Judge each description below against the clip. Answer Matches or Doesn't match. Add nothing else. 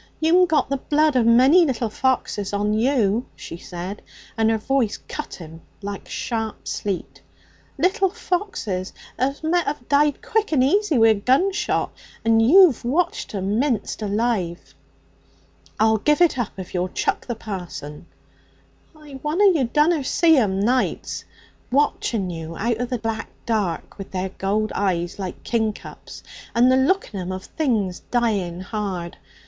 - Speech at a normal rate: Matches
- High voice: Matches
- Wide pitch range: Matches